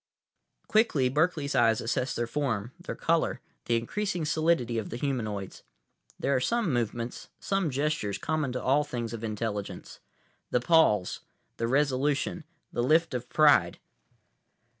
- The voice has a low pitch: Yes, low, 130 Hz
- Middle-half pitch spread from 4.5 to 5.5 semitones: Yes, average, 5.1 semitones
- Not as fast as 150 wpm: Yes, average, 140 wpm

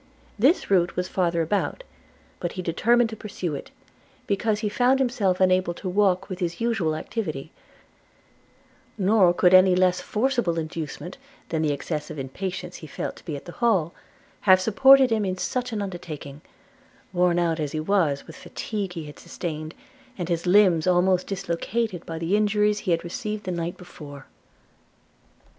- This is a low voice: No, medium, 185 Hz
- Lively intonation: No, average, 3.8 semitones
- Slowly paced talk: No, average, 165 wpm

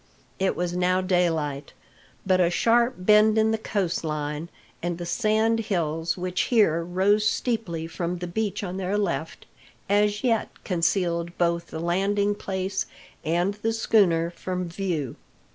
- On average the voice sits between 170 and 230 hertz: Yes, medium, 185 Hz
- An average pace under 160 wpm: Yes, average, 145 wpm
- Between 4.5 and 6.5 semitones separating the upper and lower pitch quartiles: No, average, 3.5 semitones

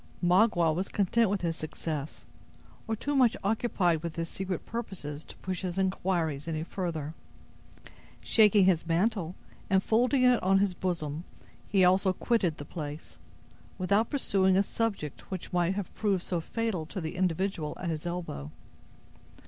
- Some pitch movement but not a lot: Yes, average, 3.5 semitones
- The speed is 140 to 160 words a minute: Yes, average, 155 wpm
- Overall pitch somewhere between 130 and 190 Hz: Yes, medium, 185 Hz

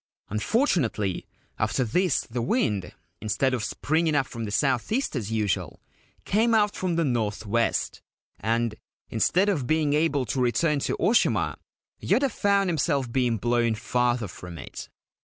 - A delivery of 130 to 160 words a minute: Yes, average, 150 wpm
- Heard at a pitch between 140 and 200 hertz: No, low, 125 Hz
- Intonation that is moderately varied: No, wide, 6.8 semitones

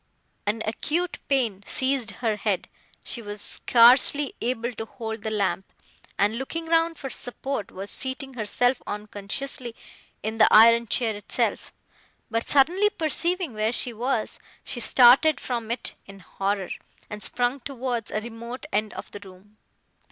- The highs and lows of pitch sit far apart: No, average, 3.9 semitones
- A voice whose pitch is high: Yes, high, 235 Hz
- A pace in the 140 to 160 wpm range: Yes, average, 145 wpm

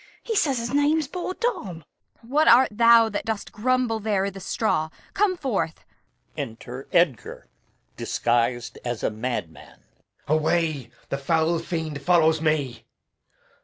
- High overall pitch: No, medium, 175 Hz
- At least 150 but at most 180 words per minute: No, average, 140 wpm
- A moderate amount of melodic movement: No, wide, 8.8 semitones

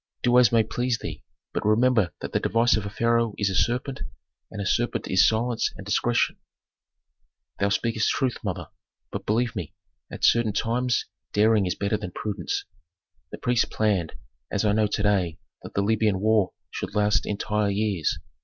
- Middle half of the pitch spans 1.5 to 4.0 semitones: Yes, narrow, 2.6 semitones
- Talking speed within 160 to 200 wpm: Yes, average, 175 wpm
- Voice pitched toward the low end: Yes, low, 110 Hz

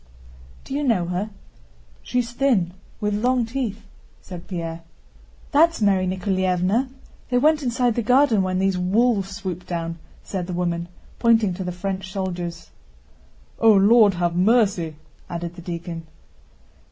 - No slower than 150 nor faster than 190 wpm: No, average, 140 wpm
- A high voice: Yes, high, 195 Hz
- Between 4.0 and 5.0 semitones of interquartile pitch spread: Yes, average, 4.7 semitones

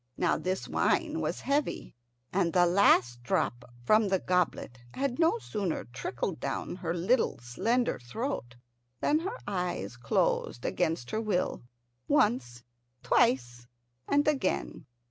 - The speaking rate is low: Yes, slow, 125 wpm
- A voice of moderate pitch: Yes, medium, 180 Hz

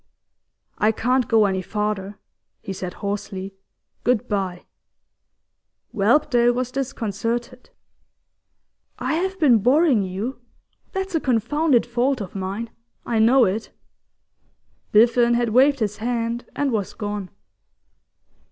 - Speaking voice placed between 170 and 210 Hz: No, high, 230 Hz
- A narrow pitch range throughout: No, average, 3.6 semitones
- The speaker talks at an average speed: No, slow, 115 wpm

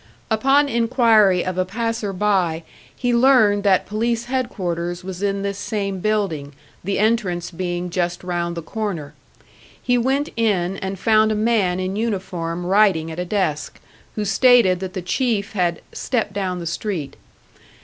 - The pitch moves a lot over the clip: No, average, 3.8 semitones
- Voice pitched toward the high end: Yes, high, 195 Hz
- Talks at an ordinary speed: Yes, average, 155 wpm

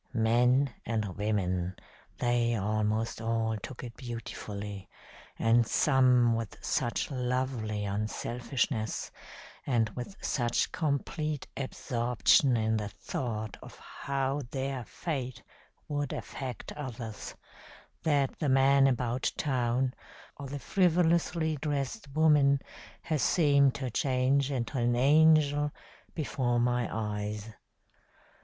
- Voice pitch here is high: No, low, 125 Hz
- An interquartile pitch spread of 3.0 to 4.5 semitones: Yes, average, 3.7 semitones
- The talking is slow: Yes, slow, 105 wpm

